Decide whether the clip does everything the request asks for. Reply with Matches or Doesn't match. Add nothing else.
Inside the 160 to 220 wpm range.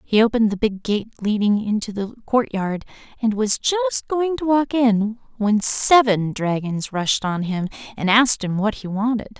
Matches